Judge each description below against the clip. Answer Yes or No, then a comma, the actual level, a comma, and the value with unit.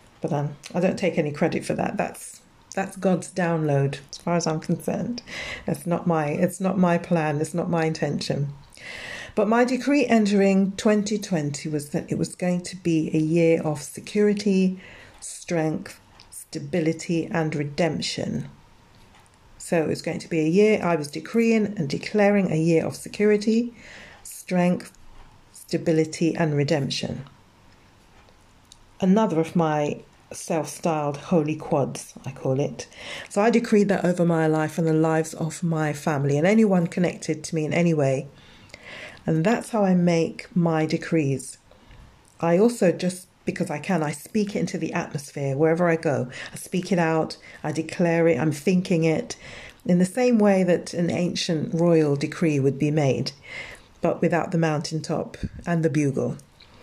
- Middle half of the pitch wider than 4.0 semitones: No, average, 3.2 semitones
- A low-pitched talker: No, medium, 165 Hz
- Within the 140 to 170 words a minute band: Yes, average, 160 wpm